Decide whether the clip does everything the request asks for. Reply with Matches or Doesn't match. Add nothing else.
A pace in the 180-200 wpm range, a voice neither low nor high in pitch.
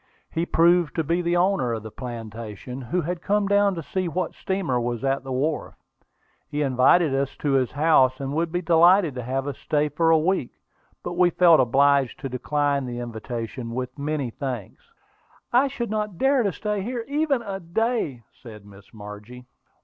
Matches